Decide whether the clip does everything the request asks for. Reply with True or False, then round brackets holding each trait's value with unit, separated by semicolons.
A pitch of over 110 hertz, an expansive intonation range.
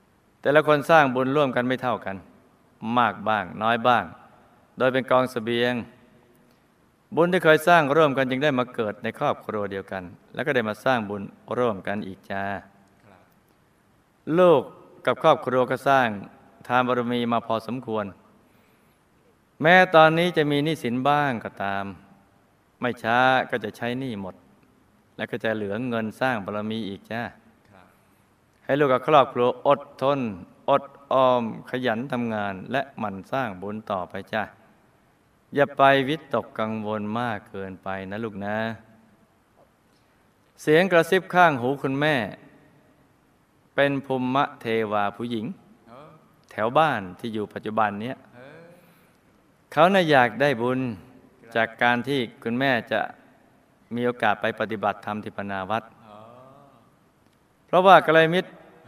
False (120 Hz; 4.7 semitones)